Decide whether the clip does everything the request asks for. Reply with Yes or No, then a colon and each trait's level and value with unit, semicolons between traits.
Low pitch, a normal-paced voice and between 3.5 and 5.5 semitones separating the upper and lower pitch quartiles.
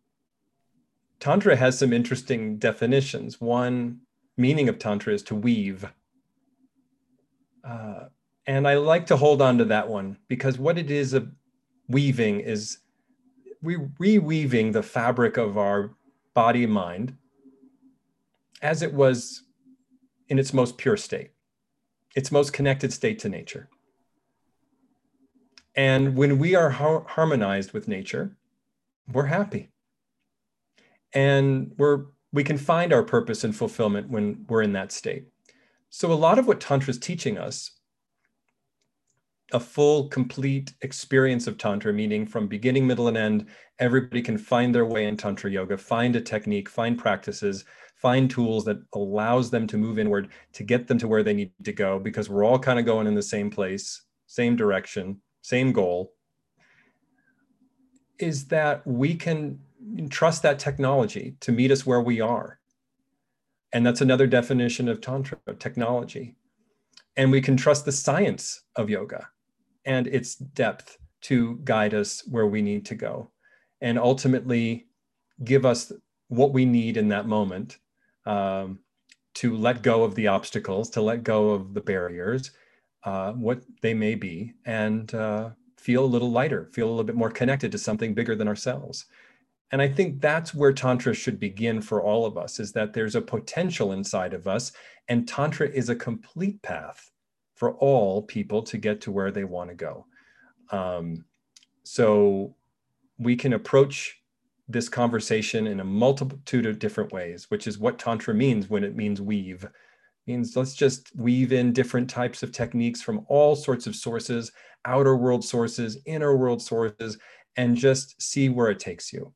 Yes: low, 125 Hz; average, 160 wpm; average, 4.5 semitones